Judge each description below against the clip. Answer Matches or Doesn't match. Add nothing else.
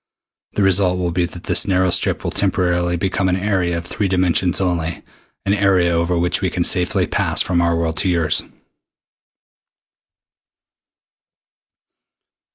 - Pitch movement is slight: Matches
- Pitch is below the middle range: Matches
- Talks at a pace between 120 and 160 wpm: Matches